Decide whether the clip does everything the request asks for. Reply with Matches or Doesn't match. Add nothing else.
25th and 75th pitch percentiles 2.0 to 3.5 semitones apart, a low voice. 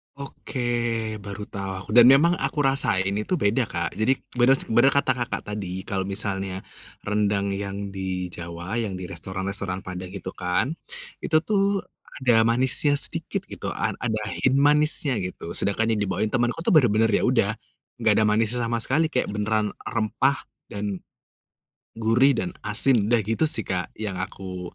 Doesn't match